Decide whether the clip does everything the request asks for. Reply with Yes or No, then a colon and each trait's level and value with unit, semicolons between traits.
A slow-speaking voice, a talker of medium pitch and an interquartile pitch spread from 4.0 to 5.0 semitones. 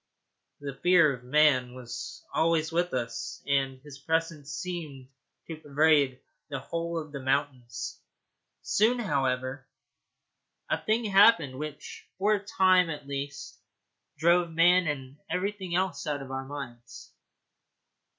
Yes: slow, 130 wpm; medium, 150 Hz; average, 4.3 semitones